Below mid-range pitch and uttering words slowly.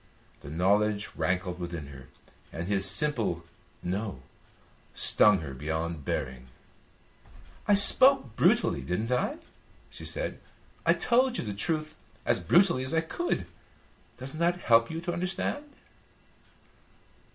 Yes: low, 105 Hz; slow, 125 wpm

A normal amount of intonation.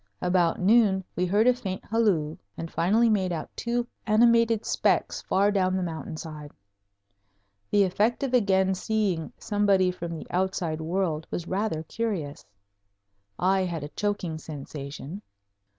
Yes: average, 4.2 semitones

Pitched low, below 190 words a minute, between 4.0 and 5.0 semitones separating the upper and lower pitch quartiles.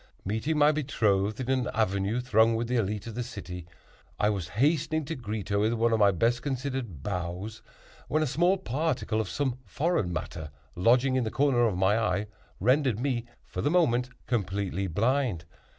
Yes: low, 115 Hz; average, 180 wpm; average, 4.7 semitones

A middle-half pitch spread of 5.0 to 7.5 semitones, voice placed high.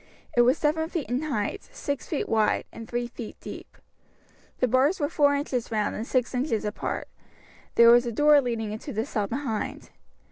No: average, 4.2 semitones; high, 245 Hz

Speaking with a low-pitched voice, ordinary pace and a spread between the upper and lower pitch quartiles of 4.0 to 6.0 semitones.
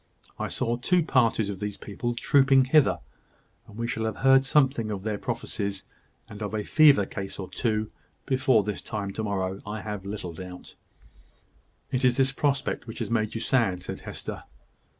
Yes: low, 110 Hz; average, 180 wpm; average, 4.4 semitones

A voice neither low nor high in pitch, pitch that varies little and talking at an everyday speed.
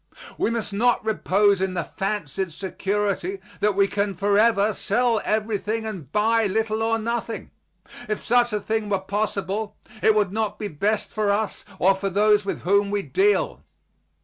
No: high, 210 Hz; narrow, 1.8 semitones; average, 165 wpm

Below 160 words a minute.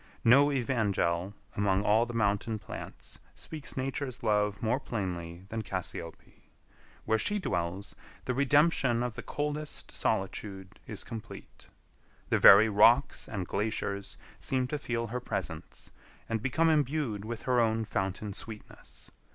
Yes: slow, 135 wpm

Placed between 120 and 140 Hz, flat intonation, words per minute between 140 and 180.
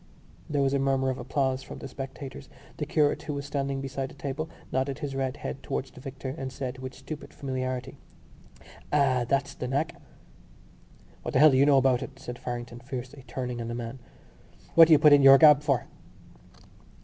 No: low, 135 Hz; narrow, 1.5 semitones; average, 195 wpm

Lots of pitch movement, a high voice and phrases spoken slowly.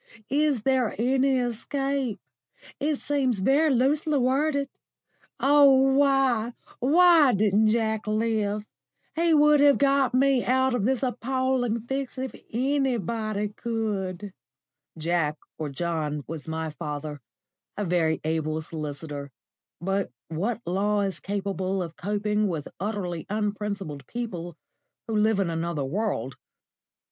Yes: wide, 7.0 semitones; high, 215 Hz; slow, 120 wpm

